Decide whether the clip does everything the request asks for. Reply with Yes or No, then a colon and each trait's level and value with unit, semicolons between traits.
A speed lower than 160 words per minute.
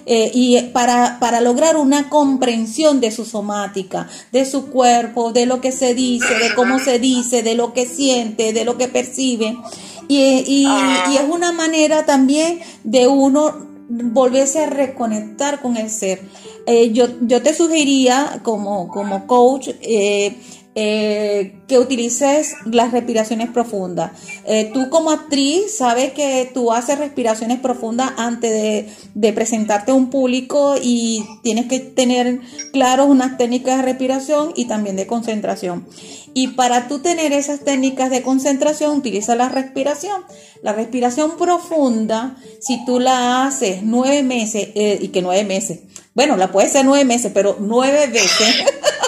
Yes: average, 150 wpm